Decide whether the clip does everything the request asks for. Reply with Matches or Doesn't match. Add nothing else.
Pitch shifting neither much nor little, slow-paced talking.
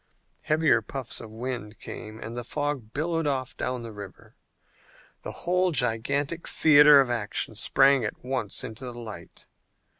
Doesn't match